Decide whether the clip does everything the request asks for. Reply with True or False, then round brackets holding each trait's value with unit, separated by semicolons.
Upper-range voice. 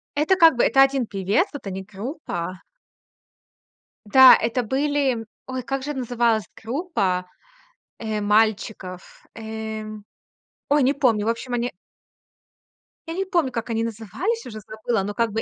True (230 Hz)